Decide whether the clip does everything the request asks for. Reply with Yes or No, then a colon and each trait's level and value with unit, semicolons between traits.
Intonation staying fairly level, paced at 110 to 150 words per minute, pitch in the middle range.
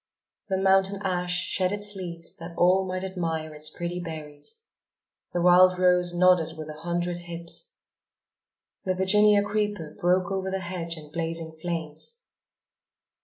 Yes: narrow, 2.3 semitones; average, 140 wpm; medium, 180 Hz